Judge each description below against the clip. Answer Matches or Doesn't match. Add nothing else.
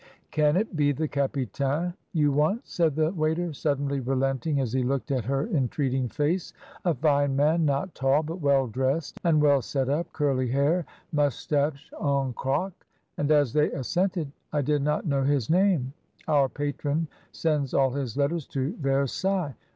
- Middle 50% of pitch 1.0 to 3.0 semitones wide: Matches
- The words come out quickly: Doesn't match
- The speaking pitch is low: Doesn't match